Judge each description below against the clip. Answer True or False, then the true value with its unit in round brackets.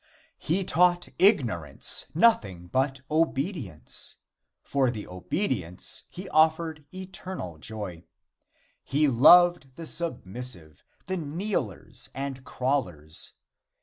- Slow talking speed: True (90 wpm)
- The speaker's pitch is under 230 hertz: True (140 Hz)